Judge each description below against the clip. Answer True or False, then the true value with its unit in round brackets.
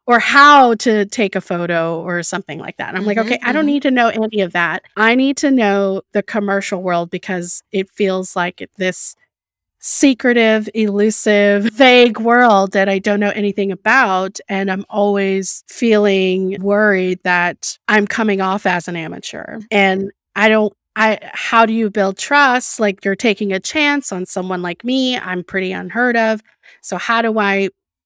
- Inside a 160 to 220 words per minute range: True (175 wpm)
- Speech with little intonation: False (3.2 semitones)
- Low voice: False (205 Hz)